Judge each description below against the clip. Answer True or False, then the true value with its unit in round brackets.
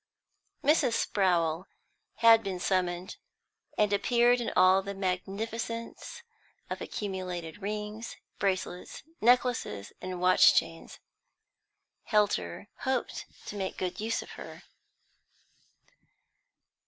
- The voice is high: True (200 Hz)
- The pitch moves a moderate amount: True (3.8 semitones)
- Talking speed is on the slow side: True (95 wpm)